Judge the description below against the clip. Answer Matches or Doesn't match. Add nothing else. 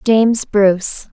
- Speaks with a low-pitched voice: Doesn't match